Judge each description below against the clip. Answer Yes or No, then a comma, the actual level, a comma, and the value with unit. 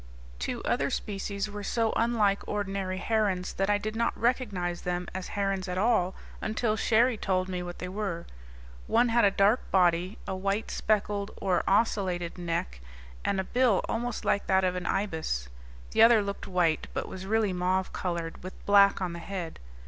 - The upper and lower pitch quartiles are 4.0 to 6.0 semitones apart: No, average, 2.8 semitones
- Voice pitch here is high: Yes, high, 195 Hz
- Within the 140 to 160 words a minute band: No, average, 180 wpm